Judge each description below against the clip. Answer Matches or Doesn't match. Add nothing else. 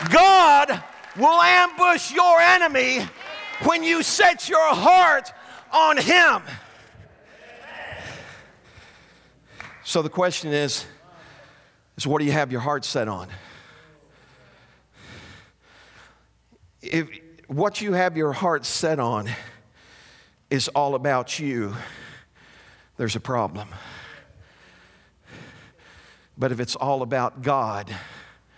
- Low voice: Doesn't match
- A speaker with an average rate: Doesn't match